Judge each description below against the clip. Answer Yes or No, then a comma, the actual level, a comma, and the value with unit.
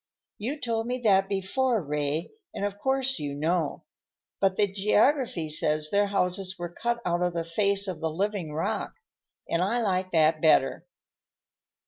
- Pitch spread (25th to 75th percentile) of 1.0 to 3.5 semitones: No, average, 4.2 semitones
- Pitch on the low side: No, high, 190 Hz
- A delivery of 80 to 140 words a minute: No, average, 160 wpm